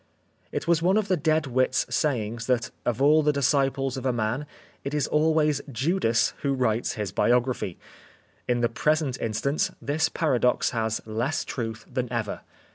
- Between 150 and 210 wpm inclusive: Yes, average, 165 wpm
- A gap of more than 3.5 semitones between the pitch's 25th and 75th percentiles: Yes, average, 4.3 semitones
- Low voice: Yes, low, 130 Hz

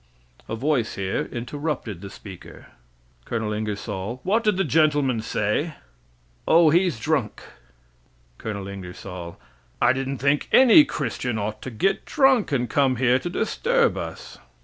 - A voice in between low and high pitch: No, low, 130 Hz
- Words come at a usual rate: Yes, average, 145 wpm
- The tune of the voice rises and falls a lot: Yes, wide, 7.1 semitones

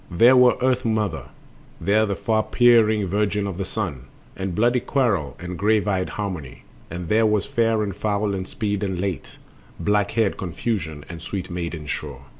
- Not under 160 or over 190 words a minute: Yes, average, 175 wpm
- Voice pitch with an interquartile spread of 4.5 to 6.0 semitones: No, average, 3.4 semitones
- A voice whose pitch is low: Yes, low, 100 Hz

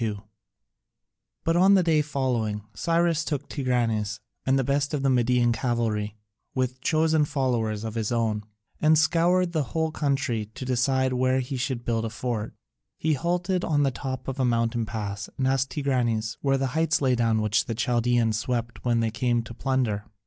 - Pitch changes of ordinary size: Yes, average, 3.8 semitones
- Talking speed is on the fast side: No, average, 180 wpm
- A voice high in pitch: No, low, 125 Hz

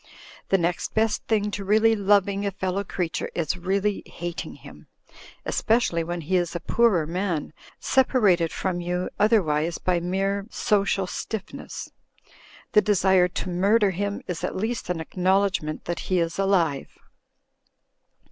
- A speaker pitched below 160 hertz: No, high, 190 Hz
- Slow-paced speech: No, average, 145 wpm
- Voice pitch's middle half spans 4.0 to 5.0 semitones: No, average, 2.7 semitones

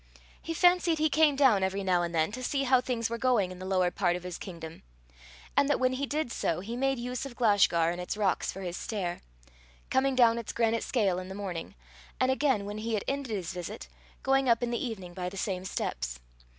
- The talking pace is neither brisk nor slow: No, fast, 230 wpm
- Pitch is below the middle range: No, high, 220 Hz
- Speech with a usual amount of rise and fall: No, wide, 6.0 semitones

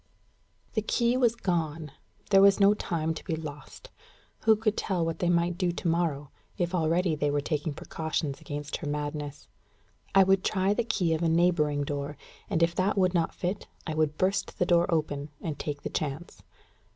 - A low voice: No, medium, 165 Hz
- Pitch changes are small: No, average, 3.8 semitones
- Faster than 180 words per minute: Yes, average, 190 wpm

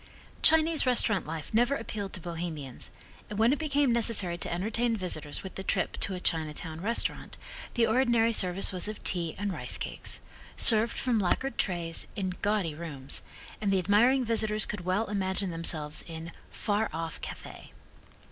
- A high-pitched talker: Yes, high, 200 Hz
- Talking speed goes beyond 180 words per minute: No, average, 165 wpm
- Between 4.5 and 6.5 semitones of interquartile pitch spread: Yes, average, 5.0 semitones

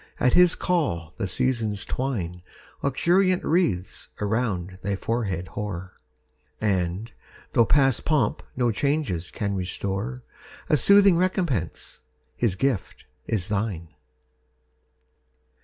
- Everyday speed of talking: No, slow, 105 wpm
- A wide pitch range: Yes, wide, 6.8 semitones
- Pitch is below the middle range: Yes, low, 110 Hz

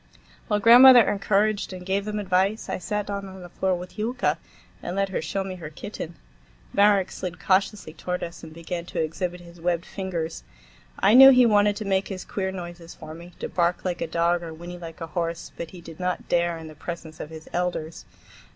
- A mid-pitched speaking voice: Yes, medium, 180 Hz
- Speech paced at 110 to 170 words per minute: No, fast, 205 wpm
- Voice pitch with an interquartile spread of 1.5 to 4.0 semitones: Yes, average, 2.8 semitones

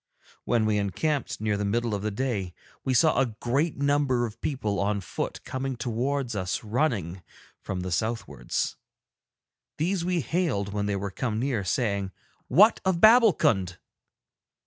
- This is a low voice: Yes, low, 115 Hz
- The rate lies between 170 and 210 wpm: No, average, 150 wpm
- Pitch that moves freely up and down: Yes, wide, 5.8 semitones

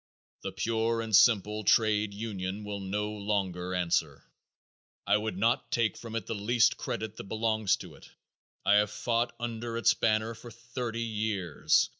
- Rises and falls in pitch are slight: Yes, narrow, 2.3 semitones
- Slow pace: No, average, 160 wpm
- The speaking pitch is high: No, low, 110 Hz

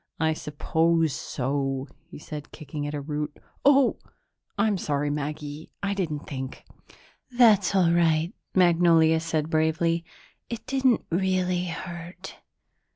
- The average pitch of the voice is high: No, medium, 165 Hz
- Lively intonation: No, average, 3.4 semitones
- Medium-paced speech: No, slow, 120 wpm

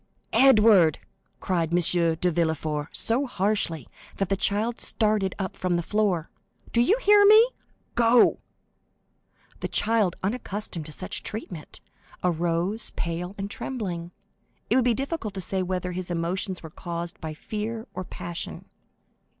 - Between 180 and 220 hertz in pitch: Yes, medium, 185 Hz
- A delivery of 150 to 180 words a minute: No, slow, 135 wpm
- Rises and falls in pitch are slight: No, average, 4.3 semitones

